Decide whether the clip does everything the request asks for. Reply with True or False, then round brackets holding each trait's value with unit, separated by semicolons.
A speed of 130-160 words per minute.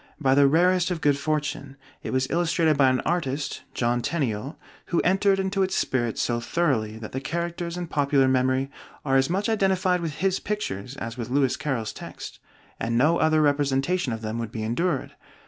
False (185 wpm)